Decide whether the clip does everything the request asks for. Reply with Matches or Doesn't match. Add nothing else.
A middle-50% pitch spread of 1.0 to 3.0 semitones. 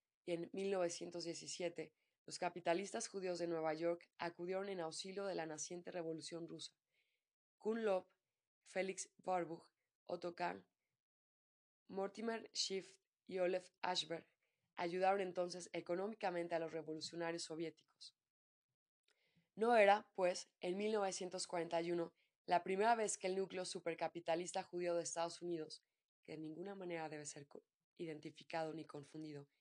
Matches